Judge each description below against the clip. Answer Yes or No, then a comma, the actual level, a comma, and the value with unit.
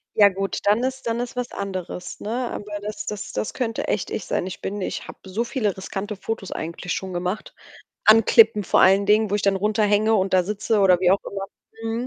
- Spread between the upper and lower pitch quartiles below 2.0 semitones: No, narrow, 2.4 semitones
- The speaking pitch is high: Yes, high, 205 Hz